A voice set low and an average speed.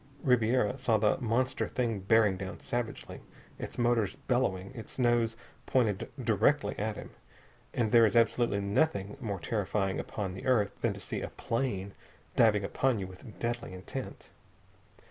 Yes: low, 110 Hz; average, 150 wpm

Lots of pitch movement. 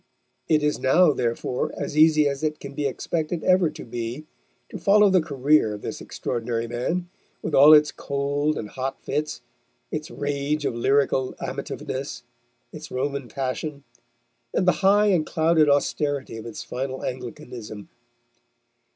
No: average, 3.3 semitones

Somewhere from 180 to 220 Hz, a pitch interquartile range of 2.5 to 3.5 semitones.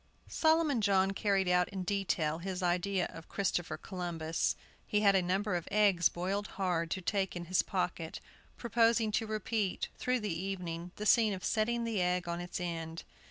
Yes: high, 190 Hz; average, 3.1 semitones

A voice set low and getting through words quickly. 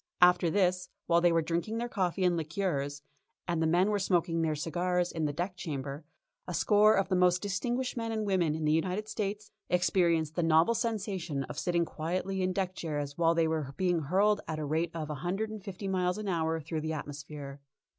No: medium, 175 Hz; fast, 210 wpm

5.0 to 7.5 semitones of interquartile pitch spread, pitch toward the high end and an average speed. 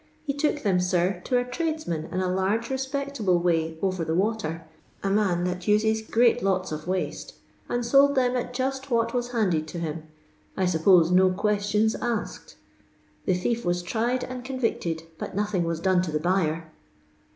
Yes: wide, 5.6 semitones; high, 195 Hz; average, 175 wpm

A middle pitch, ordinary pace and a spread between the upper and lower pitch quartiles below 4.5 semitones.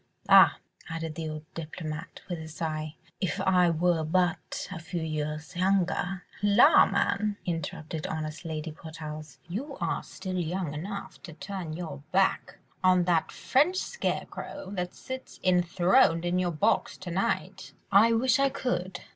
Yes: medium, 175 Hz; average, 150 wpm; average, 3.3 semitones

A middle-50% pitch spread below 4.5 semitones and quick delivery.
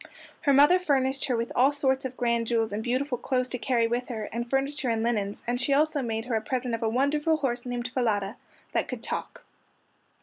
Yes: average, 2.7 semitones; fast, 215 wpm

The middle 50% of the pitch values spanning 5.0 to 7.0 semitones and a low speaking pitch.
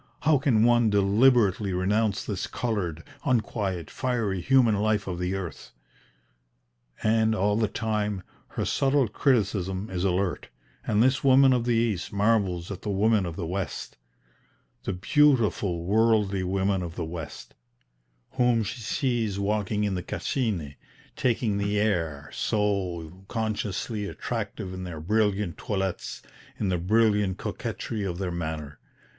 No: average, 3.3 semitones; low, 105 Hz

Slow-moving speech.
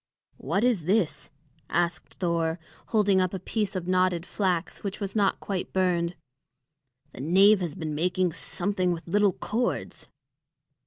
No: average, 145 wpm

